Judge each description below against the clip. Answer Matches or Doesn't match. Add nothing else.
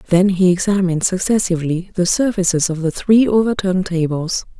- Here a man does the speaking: Doesn't match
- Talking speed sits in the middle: Matches